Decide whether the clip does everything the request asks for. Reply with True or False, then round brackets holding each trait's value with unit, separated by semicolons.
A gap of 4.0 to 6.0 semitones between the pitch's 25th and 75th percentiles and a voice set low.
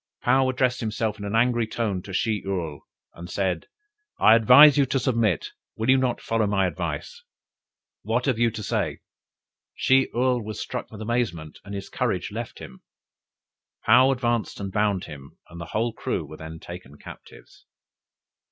True (4.4 semitones; 110 Hz)